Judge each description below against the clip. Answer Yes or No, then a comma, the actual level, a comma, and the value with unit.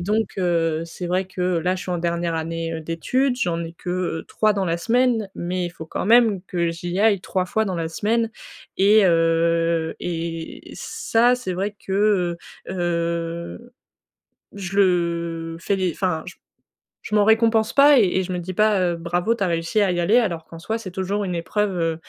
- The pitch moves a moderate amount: Yes, average, 3.7 semitones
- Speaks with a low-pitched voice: No, medium, 180 Hz